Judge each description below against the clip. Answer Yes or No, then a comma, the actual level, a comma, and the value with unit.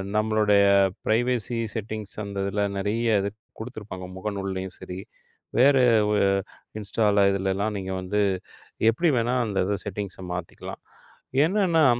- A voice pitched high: No, low, 105 Hz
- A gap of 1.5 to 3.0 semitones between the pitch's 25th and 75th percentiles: Yes, average, 2.7 semitones